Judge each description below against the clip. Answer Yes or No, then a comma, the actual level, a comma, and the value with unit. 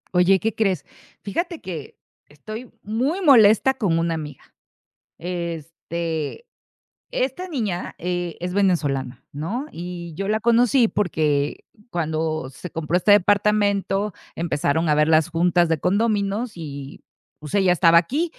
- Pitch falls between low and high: Yes, medium, 180 Hz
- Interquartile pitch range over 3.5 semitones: Yes, average, 4.8 semitones